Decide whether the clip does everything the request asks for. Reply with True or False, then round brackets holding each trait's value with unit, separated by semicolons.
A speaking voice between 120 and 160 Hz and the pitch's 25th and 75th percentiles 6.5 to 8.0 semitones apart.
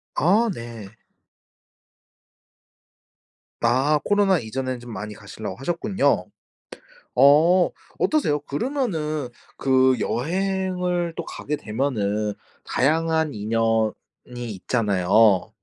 True (135 Hz; 7.3 semitones)